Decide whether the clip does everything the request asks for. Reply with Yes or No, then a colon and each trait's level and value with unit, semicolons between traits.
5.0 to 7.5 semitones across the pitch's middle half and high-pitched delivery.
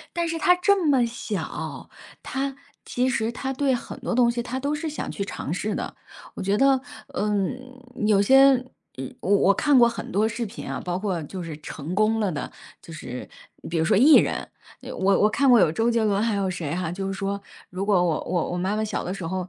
Yes: wide, 5.5 semitones; high, 215 Hz